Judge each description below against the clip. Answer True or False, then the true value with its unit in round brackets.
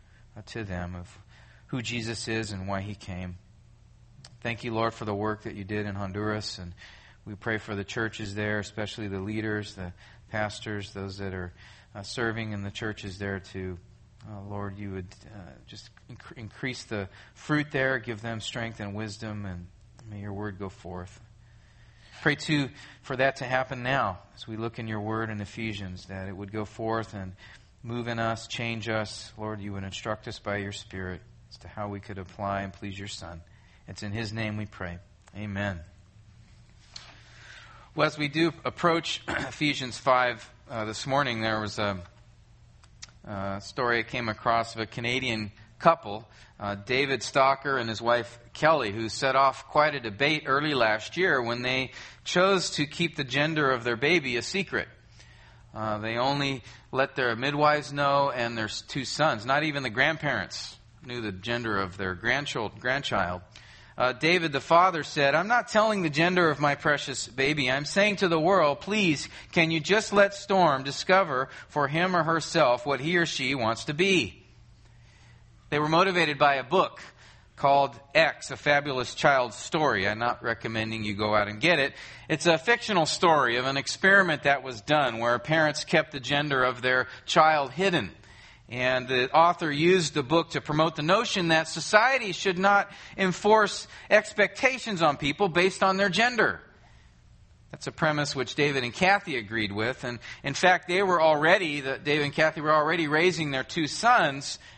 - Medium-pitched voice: False (120 Hz)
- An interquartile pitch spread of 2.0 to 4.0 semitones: False (5.6 semitones)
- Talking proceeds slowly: False (175 wpm)